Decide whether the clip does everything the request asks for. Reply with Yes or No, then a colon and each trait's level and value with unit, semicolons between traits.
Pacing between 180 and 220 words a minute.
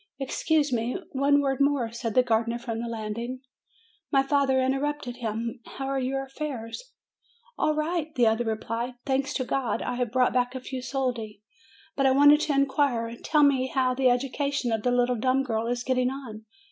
Yes: average, 190 wpm